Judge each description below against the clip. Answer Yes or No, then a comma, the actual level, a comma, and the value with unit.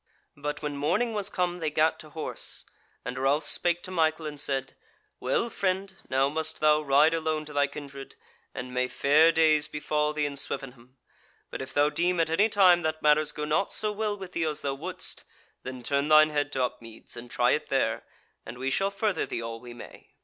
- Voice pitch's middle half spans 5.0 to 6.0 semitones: No, average, 3.2 semitones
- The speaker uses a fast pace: Yes, fast, 210 wpm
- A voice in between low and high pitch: Yes, medium, 150 Hz